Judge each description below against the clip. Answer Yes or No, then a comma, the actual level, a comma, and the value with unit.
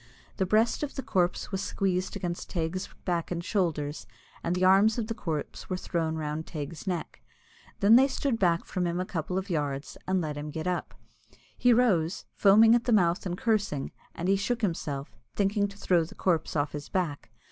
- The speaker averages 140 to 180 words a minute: No, average, 200 wpm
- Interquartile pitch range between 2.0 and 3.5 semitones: No, average, 3.9 semitones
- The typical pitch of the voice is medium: Yes, medium, 180 Hz